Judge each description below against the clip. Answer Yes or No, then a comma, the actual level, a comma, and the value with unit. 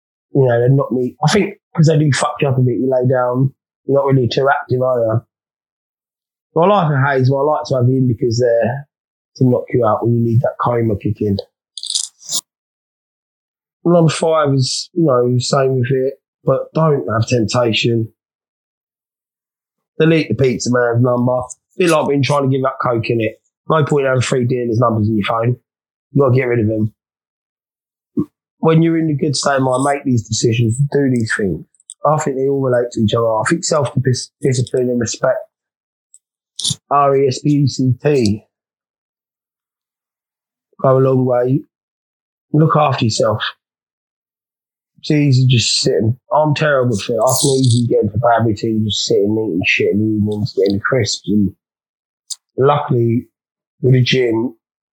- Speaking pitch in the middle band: No, low, 130 Hz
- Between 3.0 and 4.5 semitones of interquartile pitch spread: Yes, average, 3.3 semitones